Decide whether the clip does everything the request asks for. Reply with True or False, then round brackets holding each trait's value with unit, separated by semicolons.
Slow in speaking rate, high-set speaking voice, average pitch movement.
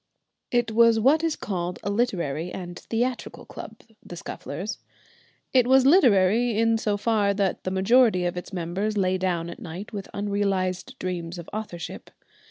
False (160 wpm; 200 Hz; 4.1 semitones)